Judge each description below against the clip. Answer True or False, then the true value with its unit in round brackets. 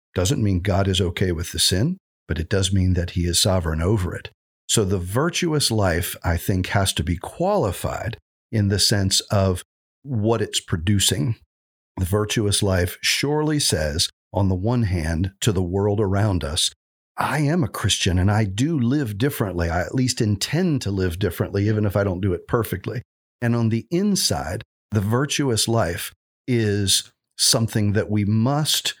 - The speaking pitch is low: True (105 Hz)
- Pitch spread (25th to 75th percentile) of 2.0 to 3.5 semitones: False (4.1 semitones)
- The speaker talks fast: False (175 wpm)